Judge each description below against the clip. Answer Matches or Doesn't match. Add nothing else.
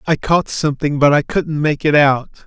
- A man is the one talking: Matches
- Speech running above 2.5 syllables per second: Matches